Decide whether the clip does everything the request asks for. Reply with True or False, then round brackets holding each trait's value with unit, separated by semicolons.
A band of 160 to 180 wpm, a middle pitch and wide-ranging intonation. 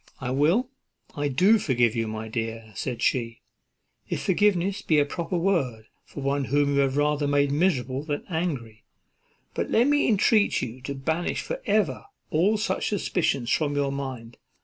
True (170 wpm; 145 Hz; 5.7 semitones)